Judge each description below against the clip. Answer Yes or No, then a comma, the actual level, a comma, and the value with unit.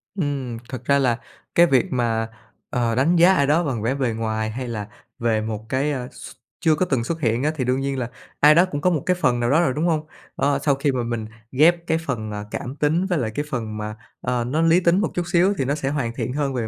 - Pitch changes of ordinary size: Yes, average, 4.8 semitones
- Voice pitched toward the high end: No, low, 135 Hz